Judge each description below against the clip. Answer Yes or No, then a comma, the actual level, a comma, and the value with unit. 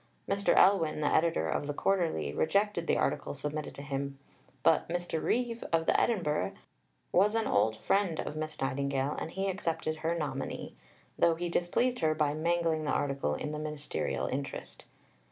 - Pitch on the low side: No, medium, 155 Hz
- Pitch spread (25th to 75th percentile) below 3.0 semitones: No, average, 3.4 semitones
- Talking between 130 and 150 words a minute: No, average, 170 wpm